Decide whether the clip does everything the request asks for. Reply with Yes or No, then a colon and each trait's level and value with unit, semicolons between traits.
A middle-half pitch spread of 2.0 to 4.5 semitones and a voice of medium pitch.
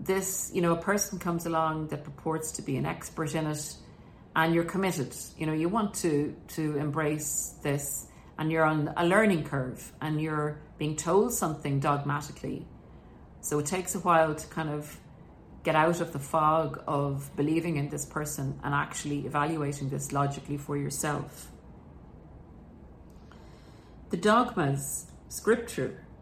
Yes: narrow, 2.4 semitones; medium, 150 Hz